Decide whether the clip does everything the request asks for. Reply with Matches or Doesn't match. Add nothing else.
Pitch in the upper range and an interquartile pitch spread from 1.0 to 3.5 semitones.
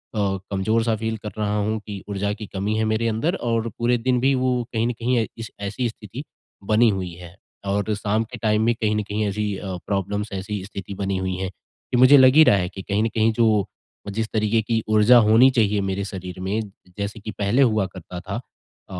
Doesn't match